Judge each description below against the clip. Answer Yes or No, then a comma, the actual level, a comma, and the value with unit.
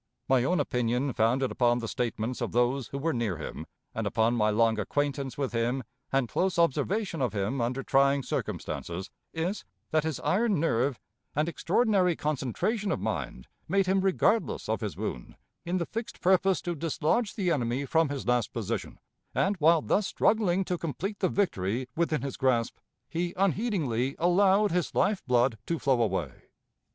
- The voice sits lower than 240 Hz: Yes, medium, 140 Hz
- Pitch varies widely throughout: Yes, wide, 6.9 semitones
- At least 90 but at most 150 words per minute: No, average, 170 wpm